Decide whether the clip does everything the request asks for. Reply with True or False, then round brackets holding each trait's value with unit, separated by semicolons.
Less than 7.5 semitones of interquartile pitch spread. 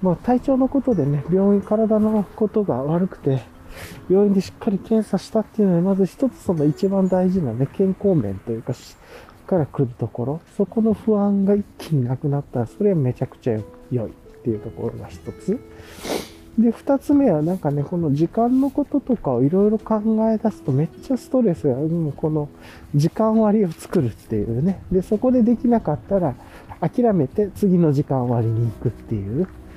False (8.2 semitones)